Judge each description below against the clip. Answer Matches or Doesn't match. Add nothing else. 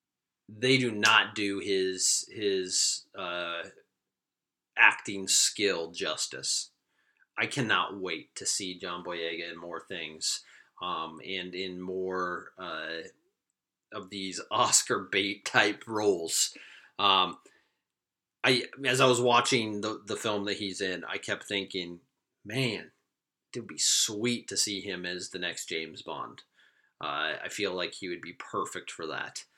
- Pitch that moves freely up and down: Doesn't match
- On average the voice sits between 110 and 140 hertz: Doesn't match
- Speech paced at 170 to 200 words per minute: Doesn't match